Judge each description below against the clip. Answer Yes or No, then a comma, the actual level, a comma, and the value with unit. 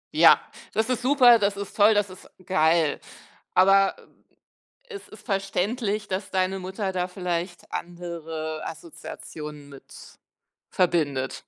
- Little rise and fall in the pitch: No, average, 3.4 semitones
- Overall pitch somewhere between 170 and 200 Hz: Yes, medium, 185 Hz